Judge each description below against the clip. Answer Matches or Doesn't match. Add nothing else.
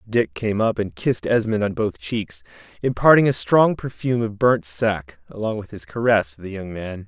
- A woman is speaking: Doesn't match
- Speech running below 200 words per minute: Doesn't match